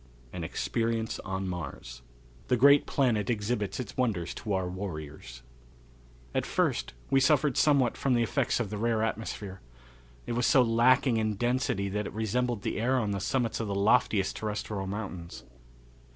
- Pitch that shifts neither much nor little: Yes, average, 3.9 semitones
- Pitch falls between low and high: No, low, 110 Hz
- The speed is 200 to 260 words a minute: No, average, 165 wpm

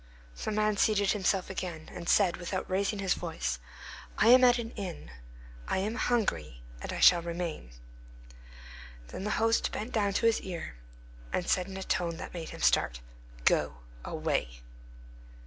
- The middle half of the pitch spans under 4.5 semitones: Yes, average, 3.9 semitones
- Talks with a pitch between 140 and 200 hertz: Yes, high, 190 Hz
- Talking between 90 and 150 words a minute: No, average, 165 wpm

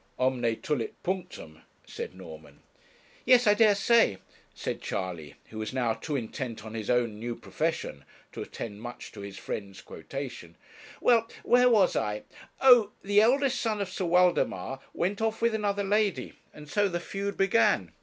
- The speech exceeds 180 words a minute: No, average, 165 wpm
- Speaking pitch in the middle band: Yes, medium, 150 Hz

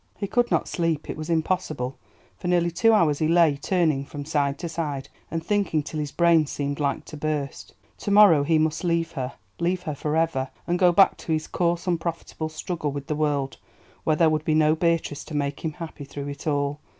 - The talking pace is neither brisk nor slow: No, fast, 215 wpm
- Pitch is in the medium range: Yes, medium, 155 Hz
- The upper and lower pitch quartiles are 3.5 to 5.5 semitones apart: No, average, 2.7 semitones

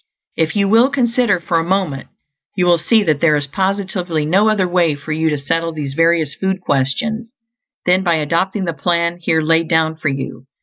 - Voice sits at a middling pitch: Yes, medium, 170 Hz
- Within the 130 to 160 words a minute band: No, average, 200 wpm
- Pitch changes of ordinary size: Yes, average, 3.5 semitones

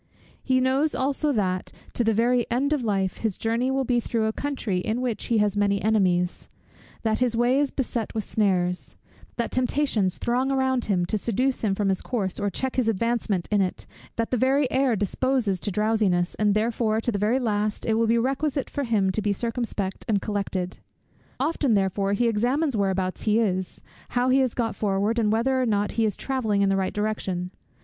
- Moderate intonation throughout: Yes, average, 4.0 semitones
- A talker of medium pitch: No, high, 220 Hz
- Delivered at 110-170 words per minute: No, fast, 205 wpm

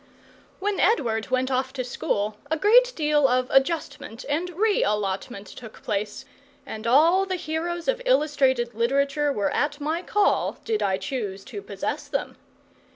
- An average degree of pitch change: No, wide, 6.9 semitones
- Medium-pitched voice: No, very high, 275 Hz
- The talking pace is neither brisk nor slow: Yes, average, 155 wpm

